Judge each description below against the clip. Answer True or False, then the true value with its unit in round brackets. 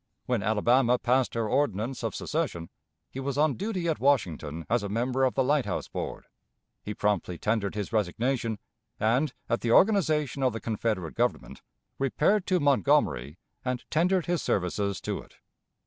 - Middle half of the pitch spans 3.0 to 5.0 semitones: False (5.4 semitones)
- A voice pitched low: True (120 Hz)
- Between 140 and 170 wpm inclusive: True (160 wpm)